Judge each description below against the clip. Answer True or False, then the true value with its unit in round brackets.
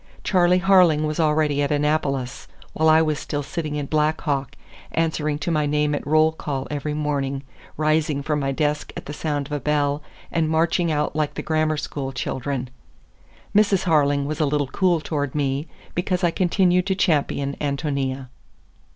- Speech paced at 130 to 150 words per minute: False (175 wpm)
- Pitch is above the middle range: False (150 Hz)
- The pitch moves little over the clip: True (1.9 semitones)